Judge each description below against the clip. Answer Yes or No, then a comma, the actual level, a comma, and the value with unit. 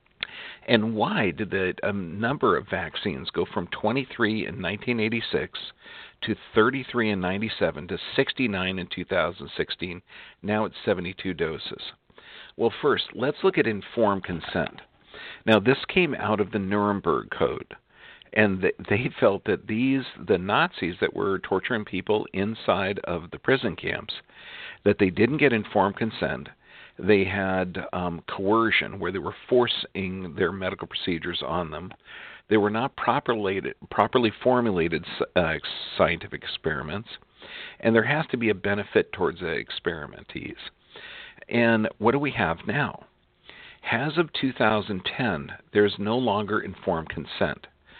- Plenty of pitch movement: No, average, 2.9 semitones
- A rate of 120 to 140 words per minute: Yes, slow, 135 wpm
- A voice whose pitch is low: Yes, low, 110 Hz